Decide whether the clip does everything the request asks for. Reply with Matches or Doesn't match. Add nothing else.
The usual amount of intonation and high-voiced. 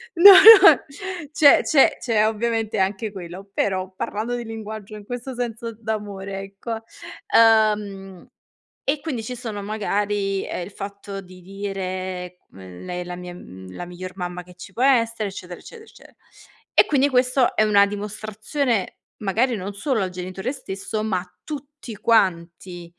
Matches